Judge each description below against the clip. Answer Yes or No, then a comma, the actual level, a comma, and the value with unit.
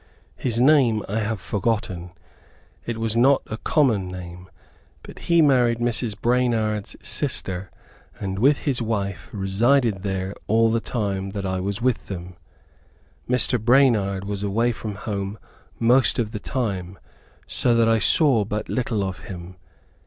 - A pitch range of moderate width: Yes, average, 3.6 semitones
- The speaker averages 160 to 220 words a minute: No, average, 145 wpm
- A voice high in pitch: No, low, 110 Hz